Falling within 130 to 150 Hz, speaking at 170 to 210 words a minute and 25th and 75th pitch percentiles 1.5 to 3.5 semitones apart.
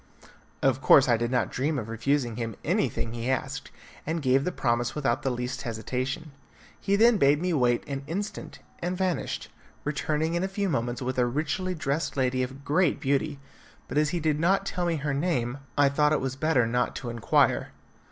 No: medium, 140 Hz; average, 195 wpm; average, 4.6 semitones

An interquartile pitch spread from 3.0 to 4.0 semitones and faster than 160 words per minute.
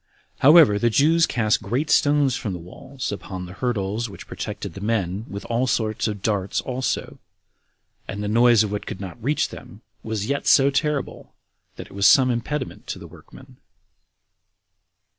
No: average, 4.8 semitones; average, 170 wpm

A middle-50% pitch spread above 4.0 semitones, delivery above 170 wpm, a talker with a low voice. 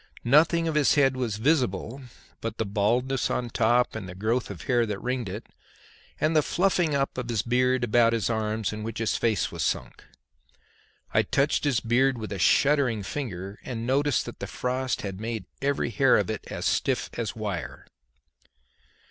No: average, 3.6 semitones; average, 185 wpm; low, 120 Hz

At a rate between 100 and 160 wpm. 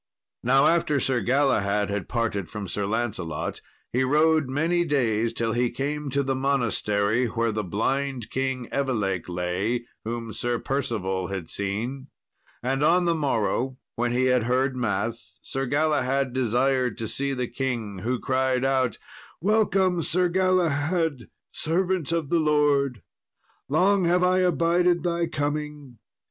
Yes: average, 140 wpm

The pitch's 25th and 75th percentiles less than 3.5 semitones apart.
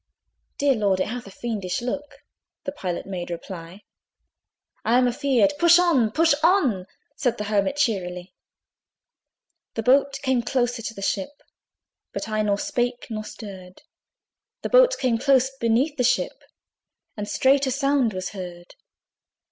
No: wide, 5.6 semitones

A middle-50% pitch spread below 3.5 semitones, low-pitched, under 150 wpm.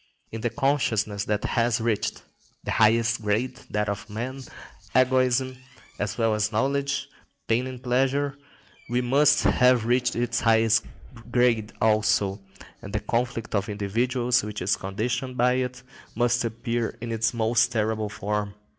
Yes: average, 2.7 semitones; low, 115 Hz; average, 140 wpm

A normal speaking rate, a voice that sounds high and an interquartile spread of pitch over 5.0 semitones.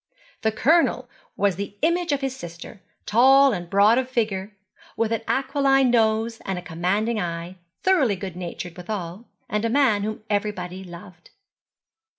Yes: average, 155 wpm; high, 210 Hz; wide, 5.5 semitones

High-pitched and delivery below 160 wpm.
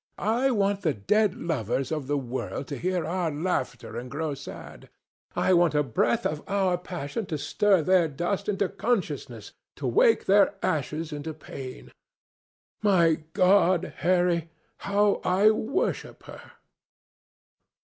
No: medium, 175 Hz; average, 140 wpm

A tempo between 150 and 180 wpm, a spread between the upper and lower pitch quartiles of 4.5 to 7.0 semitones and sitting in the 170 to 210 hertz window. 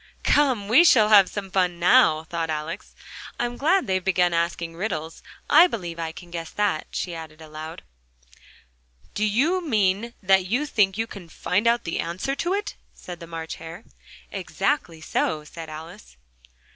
Yes: average, 165 wpm; wide, 5.5 semitones; medium, 185 Hz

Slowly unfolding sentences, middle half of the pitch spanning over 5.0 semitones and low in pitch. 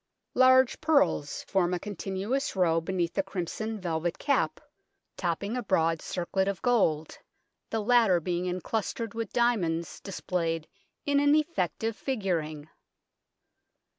No: slow, 120 wpm; wide, 5.5 semitones; high, 190 Hz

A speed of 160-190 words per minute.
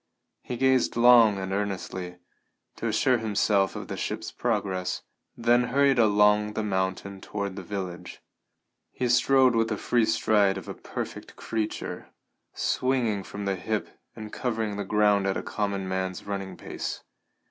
No: average, 150 wpm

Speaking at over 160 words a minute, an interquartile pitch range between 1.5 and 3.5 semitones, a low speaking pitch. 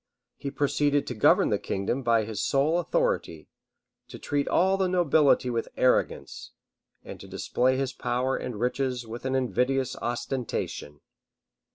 No: average, 150 wpm; average, 3.0 semitones; low, 130 Hz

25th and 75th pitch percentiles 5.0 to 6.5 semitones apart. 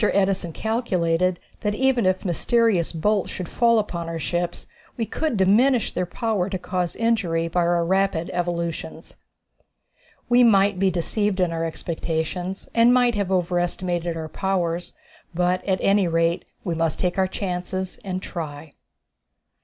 No: average, 3.1 semitones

